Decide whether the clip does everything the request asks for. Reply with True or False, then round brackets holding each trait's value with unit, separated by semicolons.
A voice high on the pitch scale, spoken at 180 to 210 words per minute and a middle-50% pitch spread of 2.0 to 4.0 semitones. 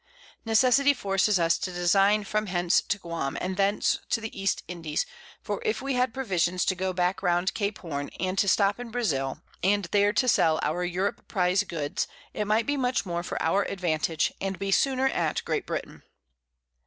True (195 Hz; 190 wpm; 3.4 semitones)